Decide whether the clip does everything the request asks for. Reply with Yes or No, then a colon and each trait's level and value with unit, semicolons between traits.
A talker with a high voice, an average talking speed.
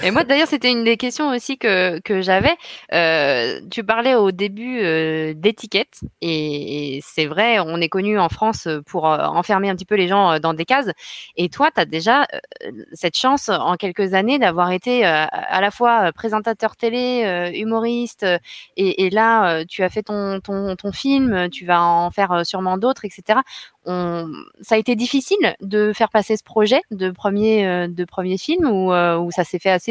Yes: high, 200 Hz; average, 205 wpm